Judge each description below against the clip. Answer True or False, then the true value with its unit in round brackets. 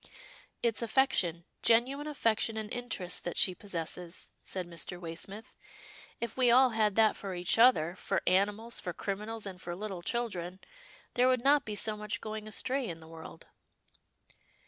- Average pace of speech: True (170 wpm)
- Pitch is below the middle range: False (210 Hz)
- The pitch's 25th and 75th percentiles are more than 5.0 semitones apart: False (4.7 semitones)